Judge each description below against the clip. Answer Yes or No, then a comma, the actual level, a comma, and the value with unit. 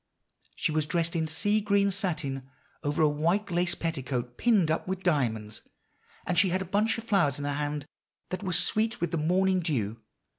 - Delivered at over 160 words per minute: Yes, average, 190 wpm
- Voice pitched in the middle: Yes, medium, 170 Hz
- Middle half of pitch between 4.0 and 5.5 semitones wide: Yes, average, 4.6 semitones